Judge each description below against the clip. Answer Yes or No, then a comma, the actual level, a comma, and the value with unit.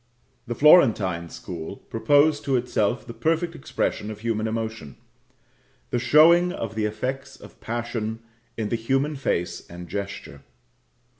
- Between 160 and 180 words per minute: No, slow, 135 wpm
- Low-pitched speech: Yes, low, 115 Hz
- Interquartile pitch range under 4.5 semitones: No, average, 4.8 semitones